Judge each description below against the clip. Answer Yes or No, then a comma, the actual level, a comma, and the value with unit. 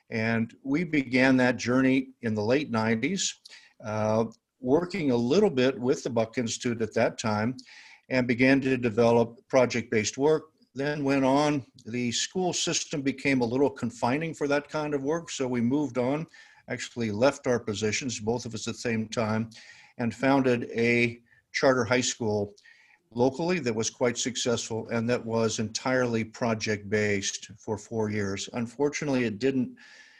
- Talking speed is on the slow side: No, average, 160 wpm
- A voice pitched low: Yes, low, 125 Hz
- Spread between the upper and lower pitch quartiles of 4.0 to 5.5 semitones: No, average, 3.2 semitones